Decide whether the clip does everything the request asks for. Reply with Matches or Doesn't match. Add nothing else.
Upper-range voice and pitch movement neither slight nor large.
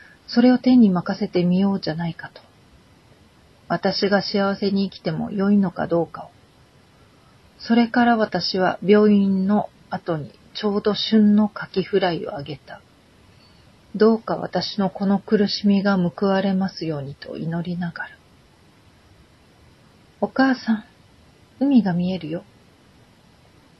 Matches